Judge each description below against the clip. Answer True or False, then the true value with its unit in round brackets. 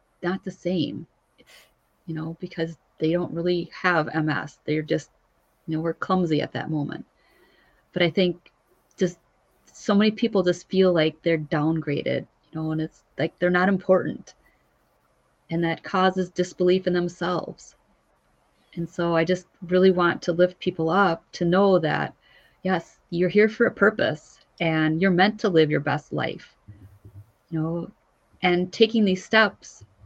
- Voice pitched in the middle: True (175 Hz)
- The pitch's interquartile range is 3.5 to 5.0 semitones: False (2.7 semitones)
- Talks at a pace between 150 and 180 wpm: True (160 wpm)